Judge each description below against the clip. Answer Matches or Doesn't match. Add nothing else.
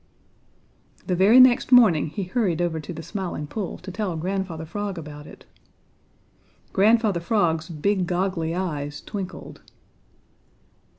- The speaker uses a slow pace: Matches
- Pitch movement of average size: Matches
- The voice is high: Doesn't match